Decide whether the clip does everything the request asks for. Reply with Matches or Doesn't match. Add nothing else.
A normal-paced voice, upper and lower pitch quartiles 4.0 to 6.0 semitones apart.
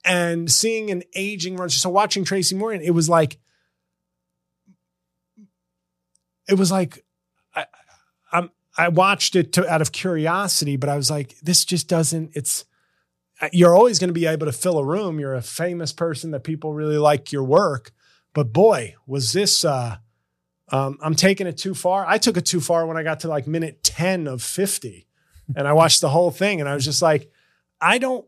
Matches